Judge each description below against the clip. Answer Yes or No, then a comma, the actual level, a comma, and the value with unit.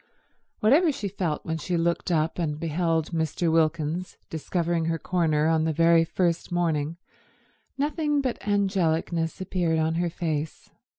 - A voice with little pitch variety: Yes, narrow, 2.1 semitones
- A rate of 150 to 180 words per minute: No, average, 140 wpm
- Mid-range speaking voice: Yes, medium, 165 Hz